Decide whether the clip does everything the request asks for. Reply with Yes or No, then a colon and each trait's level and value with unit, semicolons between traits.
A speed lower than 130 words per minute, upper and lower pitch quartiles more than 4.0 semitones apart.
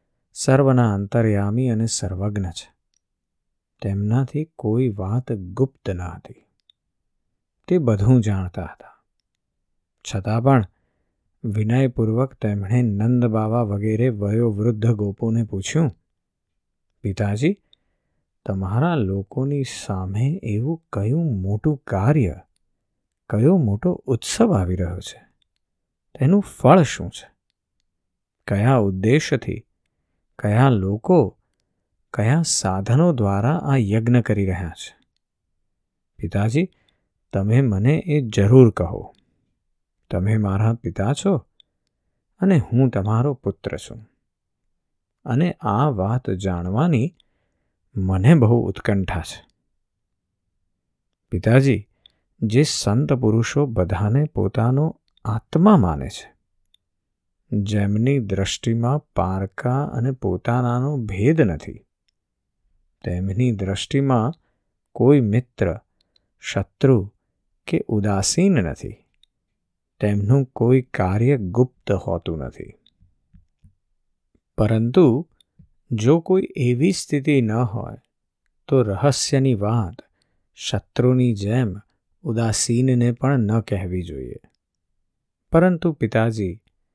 Yes: average, 90 wpm; average, 5.1 semitones